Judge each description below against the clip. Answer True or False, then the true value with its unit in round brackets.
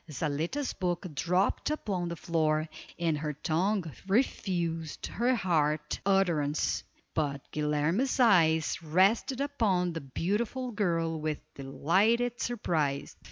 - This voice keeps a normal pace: False (110 wpm)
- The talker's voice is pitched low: False (170 Hz)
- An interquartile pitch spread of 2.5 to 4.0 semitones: False (5.1 semitones)